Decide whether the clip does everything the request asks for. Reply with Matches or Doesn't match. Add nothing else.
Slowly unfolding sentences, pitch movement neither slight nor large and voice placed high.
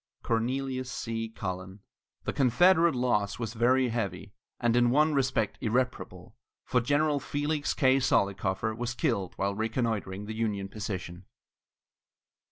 Doesn't match